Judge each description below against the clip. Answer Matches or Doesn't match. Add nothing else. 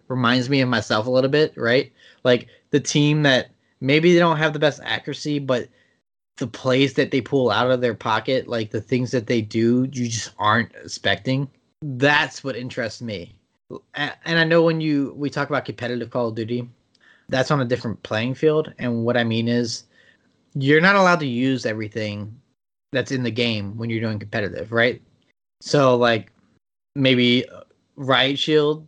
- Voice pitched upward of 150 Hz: Doesn't match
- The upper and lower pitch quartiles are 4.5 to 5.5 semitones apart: Doesn't match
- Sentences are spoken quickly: Doesn't match